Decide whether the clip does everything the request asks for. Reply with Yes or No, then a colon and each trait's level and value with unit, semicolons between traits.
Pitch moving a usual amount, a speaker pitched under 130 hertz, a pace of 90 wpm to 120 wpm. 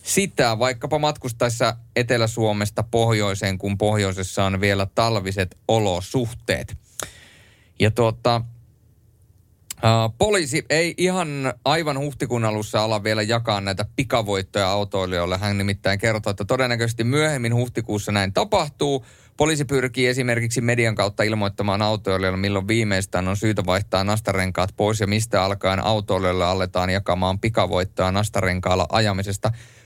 Yes: average, 3.5 semitones; low, 110 Hz; average, 115 wpm